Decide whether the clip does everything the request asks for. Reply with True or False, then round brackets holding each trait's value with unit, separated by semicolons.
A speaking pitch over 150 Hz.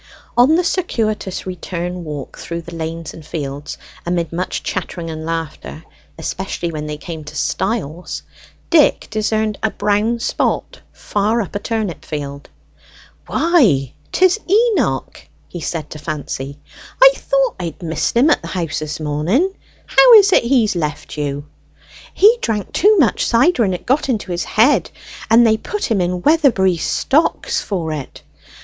True (185 Hz)